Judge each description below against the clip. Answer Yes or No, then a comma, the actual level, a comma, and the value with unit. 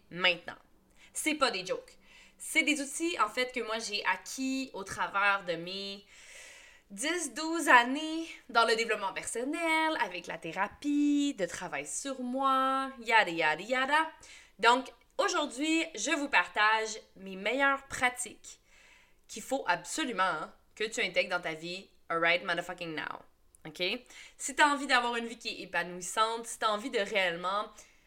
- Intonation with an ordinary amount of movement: No, wide, 7.4 semitones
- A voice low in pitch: No, high, 235 Hz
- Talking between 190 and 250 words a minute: No, average, 155 wpm